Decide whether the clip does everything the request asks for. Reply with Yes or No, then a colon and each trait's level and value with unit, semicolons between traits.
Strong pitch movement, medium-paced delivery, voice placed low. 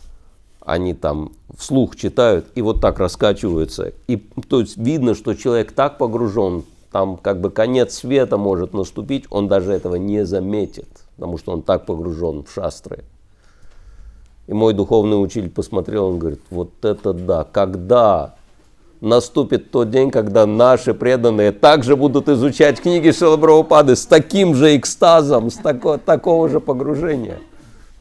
Yes: wide, 6.9 semitones; average, 140 wpm; low, 115 Hz